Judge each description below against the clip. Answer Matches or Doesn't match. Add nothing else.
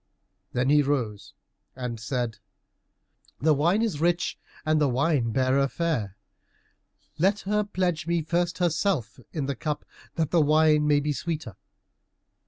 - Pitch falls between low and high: Matches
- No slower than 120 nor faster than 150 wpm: Matches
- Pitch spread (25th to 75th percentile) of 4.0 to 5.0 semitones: Matches